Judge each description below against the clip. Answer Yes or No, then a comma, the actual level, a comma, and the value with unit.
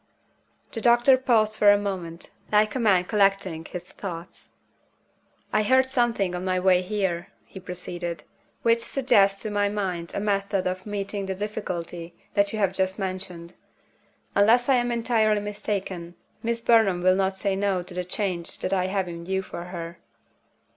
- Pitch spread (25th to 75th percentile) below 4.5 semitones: Yes, average, 2.8 semitones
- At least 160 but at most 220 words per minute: Yes, average, 170 wpm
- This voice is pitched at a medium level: No, high, 195 Hz